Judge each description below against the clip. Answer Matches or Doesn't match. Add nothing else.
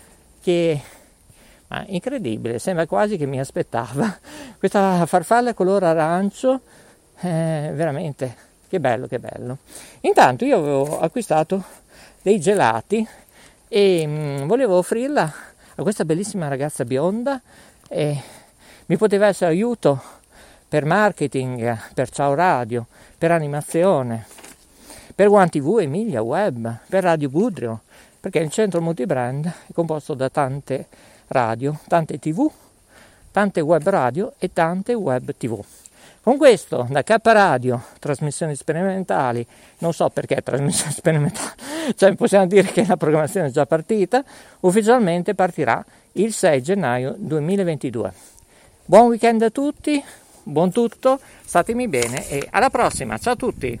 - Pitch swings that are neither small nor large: Doesn't match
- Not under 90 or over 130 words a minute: Matches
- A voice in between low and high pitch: Matches